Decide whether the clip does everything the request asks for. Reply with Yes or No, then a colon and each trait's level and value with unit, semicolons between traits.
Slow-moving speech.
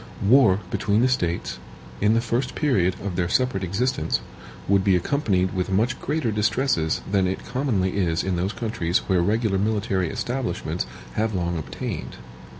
No: average, 155 wpm